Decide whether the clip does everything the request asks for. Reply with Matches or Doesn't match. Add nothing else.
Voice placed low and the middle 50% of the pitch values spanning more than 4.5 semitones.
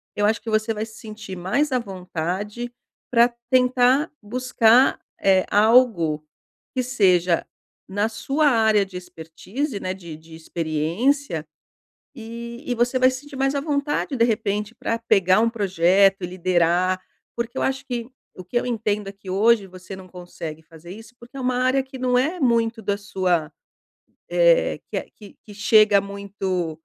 Doesn't match